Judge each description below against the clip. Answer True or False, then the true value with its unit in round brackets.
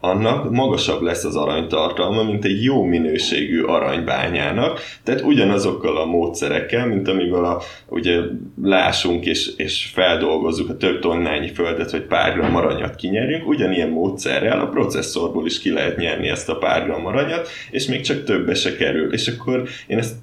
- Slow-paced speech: False (155 wpm)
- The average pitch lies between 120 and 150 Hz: False (105 Hz)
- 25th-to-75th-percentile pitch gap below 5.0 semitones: False (5.4 semitones)